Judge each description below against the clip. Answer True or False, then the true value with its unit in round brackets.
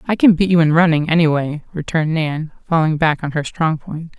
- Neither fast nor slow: False (230 wpm)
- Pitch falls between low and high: True (160 Hz)